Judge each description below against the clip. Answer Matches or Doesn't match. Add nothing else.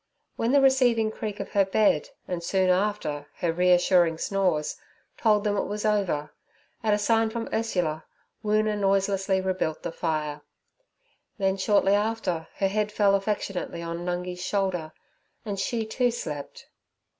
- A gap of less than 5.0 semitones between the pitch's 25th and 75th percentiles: Matches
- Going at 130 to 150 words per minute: Matches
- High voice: Matches